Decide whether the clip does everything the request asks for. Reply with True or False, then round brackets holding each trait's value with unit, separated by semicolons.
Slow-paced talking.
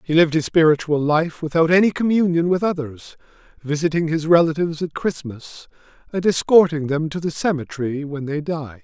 False (165 wpm)